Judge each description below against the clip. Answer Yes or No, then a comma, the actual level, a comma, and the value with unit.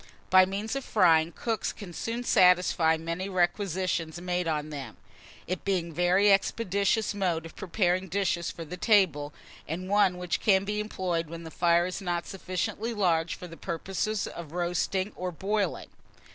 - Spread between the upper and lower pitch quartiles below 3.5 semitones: Yes, average, 2.8 semitones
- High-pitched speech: No, medium, 180 Hz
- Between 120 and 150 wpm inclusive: No, average, 165 wpm